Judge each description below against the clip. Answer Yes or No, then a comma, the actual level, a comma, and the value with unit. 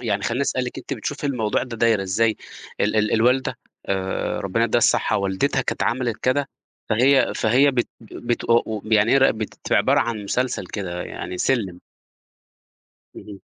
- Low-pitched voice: Yes, low, 115 Hz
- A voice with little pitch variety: No, average, 3.6 semitones